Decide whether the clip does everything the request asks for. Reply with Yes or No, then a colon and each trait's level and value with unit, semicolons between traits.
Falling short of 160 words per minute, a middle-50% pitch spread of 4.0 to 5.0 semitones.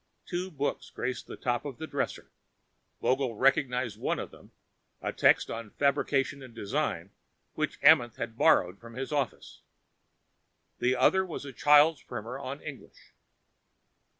No: average, 145 wpm; average, 3.5 semitones